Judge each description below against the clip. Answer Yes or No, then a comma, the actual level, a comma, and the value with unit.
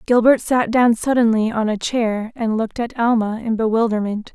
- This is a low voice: No, high, 225 Hz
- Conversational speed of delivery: Yes, average, 180 wpm